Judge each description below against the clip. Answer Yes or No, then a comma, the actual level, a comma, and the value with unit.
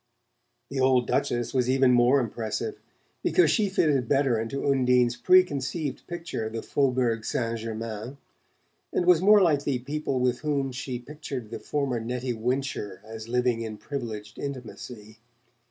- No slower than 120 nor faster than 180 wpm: Yes, average, 150 wpm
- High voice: No, low, 125 Hz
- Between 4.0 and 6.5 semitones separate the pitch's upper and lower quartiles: No, average, 3.5 semitones